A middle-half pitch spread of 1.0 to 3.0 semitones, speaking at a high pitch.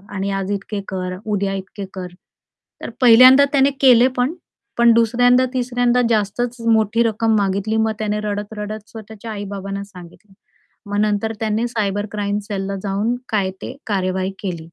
Yes: average, 2.7 semitones; high, 210 Hz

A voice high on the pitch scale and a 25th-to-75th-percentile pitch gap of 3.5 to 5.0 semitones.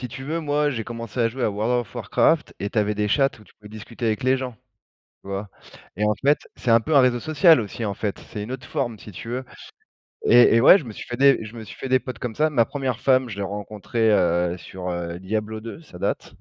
No: low, 115 Hz; average, 3.8 semitones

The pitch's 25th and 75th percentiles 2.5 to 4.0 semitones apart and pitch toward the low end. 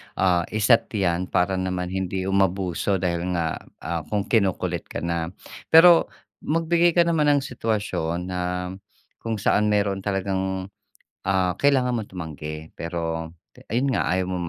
Yes: average, 3.7 semitones; very low, 95 Hz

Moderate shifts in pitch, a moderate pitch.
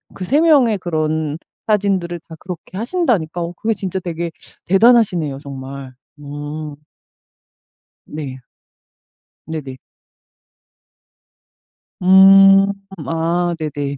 Yes: average, 4.4 semitones; medium, 170 Hz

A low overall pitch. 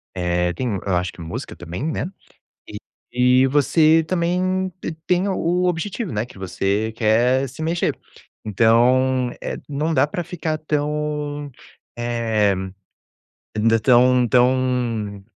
Yes: low, 130 Hz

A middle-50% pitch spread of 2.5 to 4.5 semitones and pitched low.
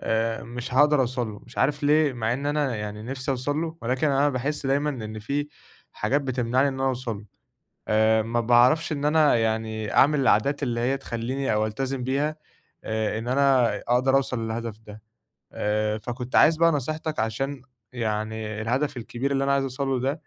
Yes: average, 3.8 semitones; low, 125 Hz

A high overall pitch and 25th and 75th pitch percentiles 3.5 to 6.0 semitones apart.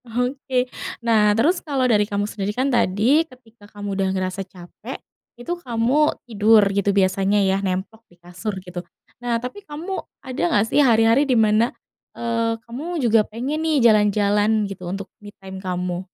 Yes: high, 220 Hz; average, 4.0 semitones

